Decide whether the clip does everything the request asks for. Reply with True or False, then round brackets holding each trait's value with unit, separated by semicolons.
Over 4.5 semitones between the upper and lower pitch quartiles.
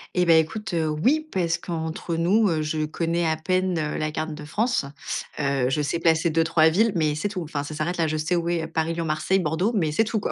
False (2.5 semitones)